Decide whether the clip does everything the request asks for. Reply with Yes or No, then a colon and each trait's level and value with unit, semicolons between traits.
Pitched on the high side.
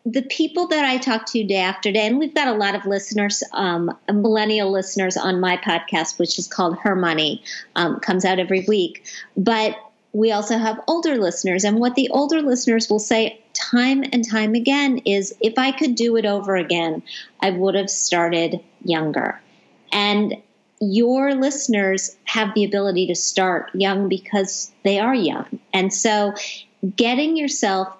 Yes: high, 210 Hz